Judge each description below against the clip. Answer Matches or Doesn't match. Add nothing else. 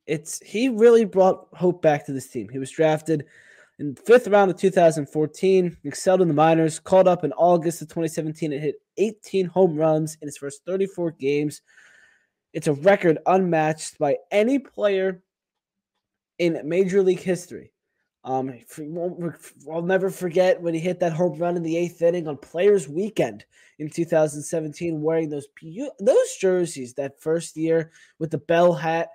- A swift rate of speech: Doesn't match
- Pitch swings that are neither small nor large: Matches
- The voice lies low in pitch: Doesn't match